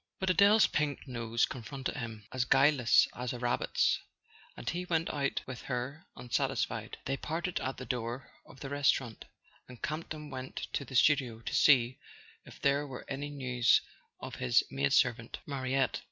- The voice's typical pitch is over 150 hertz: No, low, 130 Hz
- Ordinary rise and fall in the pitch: Yes, average, 3.1 semitones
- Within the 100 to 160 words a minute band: No, average, 170 wpm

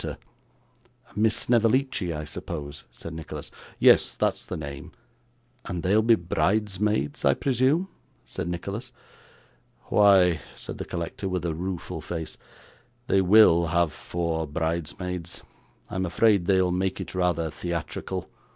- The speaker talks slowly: Yes, slow, 125 wpm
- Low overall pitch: Yes, very low, 90 Hz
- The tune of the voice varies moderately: Yes, average, 3.9 semitones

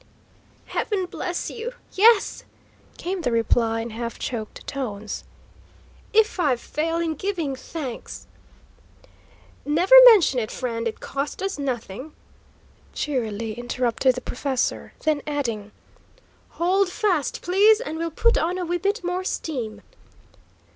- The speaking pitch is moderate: No, very high, 295 Hz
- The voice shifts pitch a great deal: Yes, wide, 7.2 semitones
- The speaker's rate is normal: No, slow, 125 wpm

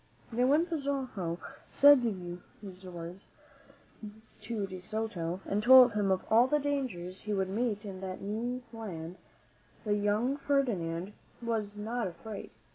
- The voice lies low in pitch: No, high, 210 Hz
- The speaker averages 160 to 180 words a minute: No, slow, 135 wpm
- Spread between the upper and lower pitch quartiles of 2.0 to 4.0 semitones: No, average, 4.8 semitones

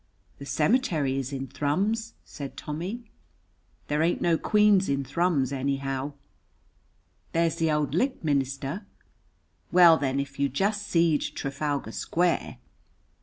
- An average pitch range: Yes, average, 4.5 semitones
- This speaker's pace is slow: Yes, slow, 120 wpm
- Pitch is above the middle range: No, medium, 150 Hz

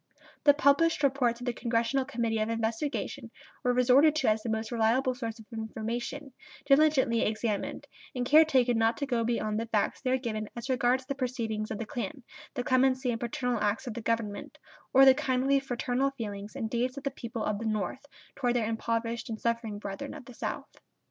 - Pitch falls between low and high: No, high, 240 Hz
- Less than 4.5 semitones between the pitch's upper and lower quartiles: Yes, average, 2.8 semitones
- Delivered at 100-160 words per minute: No, average, 195 wpm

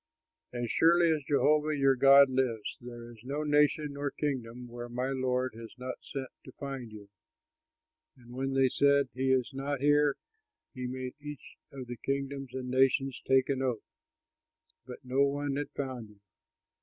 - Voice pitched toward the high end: No, low, 130 Hz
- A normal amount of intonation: No, narrow, 2.1 semitones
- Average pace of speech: Yes, average, 170 wpm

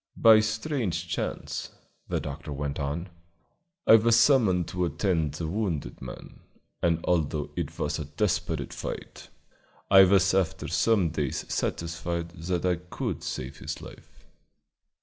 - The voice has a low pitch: Yes, very low, 85 Hz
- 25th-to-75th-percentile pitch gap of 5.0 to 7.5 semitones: No, average, 3.8 semitones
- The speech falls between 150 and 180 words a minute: No, average, 140 wpm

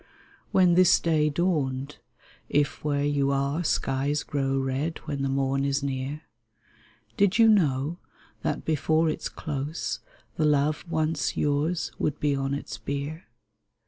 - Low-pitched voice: No, medium, 145 Hz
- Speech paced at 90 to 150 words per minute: Yes, average, 140 wpm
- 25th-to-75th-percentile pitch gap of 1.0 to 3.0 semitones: Yes, narrow, 2.4 semitones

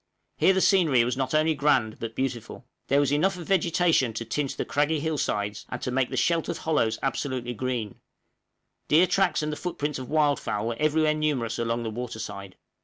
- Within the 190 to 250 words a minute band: Yes, average, 200 wpm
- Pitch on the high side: No, medium, 140 Hz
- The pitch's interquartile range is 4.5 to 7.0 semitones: Yes, average, 4.9 semitones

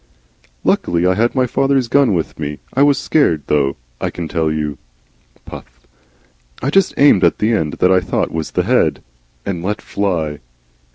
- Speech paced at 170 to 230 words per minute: Yes, average, 175 wpm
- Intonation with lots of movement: Yes, wide, 7.5 semitones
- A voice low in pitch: Yes, very low, 90 Hz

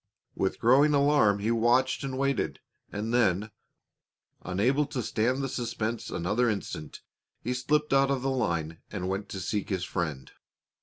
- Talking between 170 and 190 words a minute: No, average, 160 wpm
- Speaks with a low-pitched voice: Yes, low, 115 Hz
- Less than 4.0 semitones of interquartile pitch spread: No, average, 5.3 semitones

